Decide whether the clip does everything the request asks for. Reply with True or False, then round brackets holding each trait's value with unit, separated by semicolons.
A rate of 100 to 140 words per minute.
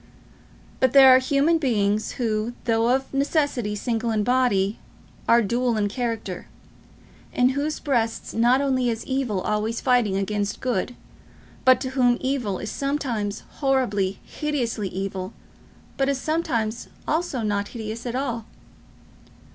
True (135 wpm)